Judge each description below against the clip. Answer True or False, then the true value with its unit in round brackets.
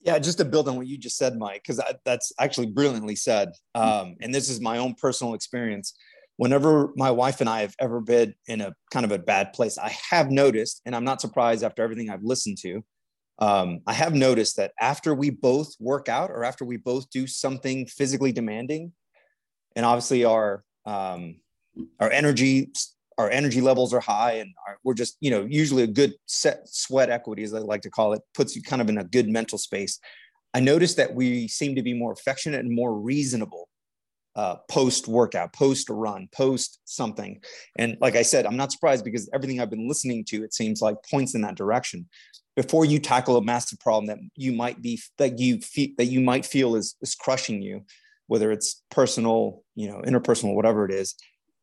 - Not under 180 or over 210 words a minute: True (205 wpm)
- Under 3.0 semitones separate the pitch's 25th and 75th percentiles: False (3.5 semitones)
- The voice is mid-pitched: False (125 Hz)